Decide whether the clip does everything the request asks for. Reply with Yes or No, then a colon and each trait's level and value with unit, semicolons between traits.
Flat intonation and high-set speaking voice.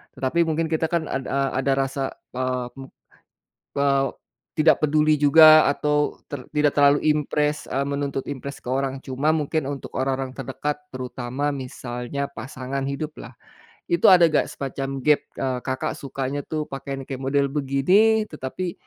No: narrow, 2.1 semitones; medium, 140 Hz